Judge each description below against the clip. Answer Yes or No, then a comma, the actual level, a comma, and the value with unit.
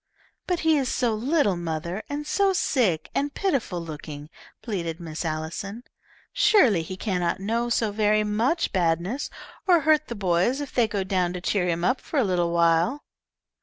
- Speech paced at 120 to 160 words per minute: No, average, 170 wpm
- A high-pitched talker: Yes, high, 205 Hz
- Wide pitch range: Yes, wide, 7.5 semitones